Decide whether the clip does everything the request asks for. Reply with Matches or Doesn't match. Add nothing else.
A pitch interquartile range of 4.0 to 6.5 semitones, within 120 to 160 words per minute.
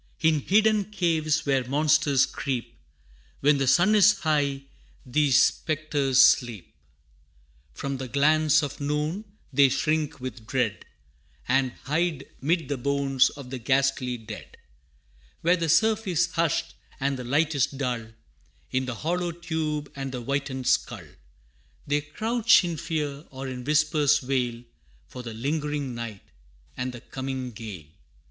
Doesn't match